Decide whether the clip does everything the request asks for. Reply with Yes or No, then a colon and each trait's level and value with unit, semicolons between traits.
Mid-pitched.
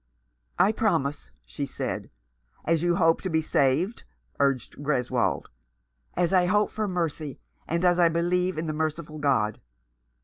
Yes: medium, 165 Hz